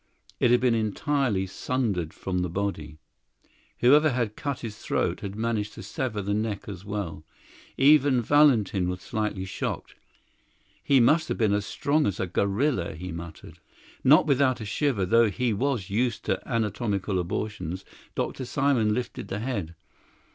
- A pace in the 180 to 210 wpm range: No, average, 155 wpm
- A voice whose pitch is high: No, low, 110 Hz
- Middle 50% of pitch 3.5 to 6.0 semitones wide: Yes, average, 4.9 semitones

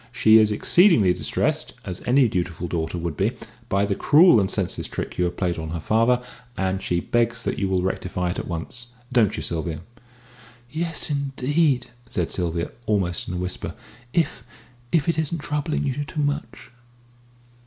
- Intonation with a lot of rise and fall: Yes, wide, 7.8 semitones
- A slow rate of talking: No, average, 170 wpm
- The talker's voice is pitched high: No, low, 105 Hz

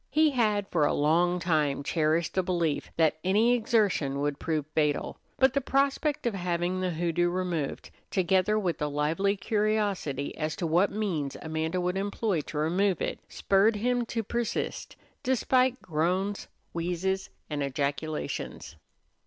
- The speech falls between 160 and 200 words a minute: No, average, 145 wpm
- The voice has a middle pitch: Yes, medium, 180 Hz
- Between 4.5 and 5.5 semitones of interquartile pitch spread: Yes, average, 4.8 semitones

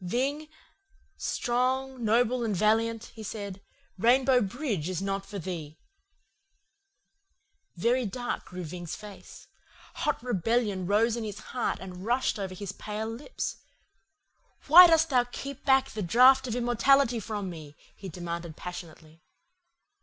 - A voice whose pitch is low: No, high, 220 Hz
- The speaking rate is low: Yes, slow, 130 wpm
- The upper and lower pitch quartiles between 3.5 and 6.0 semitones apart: Yes, average, 5.1 semitones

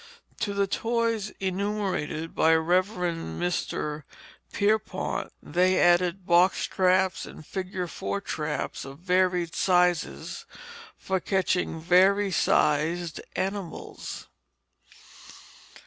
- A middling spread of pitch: No, narrow, 2.3 semitones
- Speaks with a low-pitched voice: No, medium, 180 Hz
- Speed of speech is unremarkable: No, slow, 90 wpm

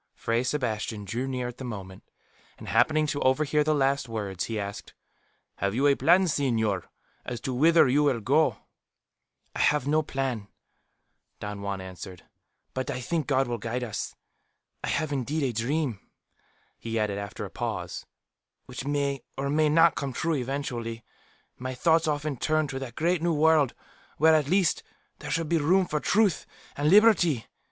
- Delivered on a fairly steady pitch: No, average, 4.9 semitones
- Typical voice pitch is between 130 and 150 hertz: Yes, low, 135 Hz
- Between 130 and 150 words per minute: No, average, 175 wpm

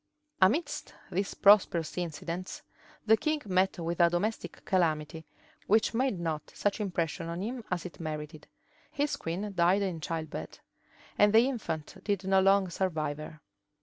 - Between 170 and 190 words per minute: No, average, 150 wpm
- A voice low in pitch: No, medium, 185 Hz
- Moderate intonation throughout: Yes, average, 3.9 semitones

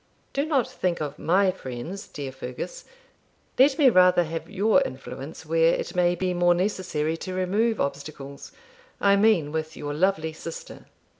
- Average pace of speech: Yes, average, 155 wpm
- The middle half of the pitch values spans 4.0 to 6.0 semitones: Yes, average, 4.3 semitones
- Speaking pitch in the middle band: Yes, medium, 175 Hz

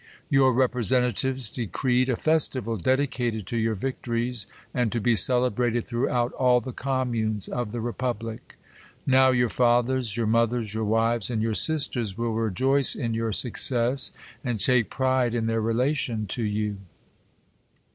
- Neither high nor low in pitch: No, low, 120 Hz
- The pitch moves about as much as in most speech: No, narrow, 2.2 semitones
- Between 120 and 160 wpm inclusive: Yes, average, 150 wpm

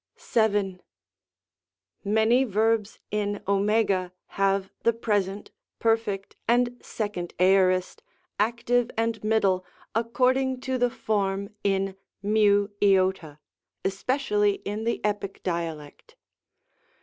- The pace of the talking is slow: Yes, slow, 90 wpm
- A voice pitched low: No, high, 205 Hz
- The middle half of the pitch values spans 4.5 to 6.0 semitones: No, narrow, 2.6 semitones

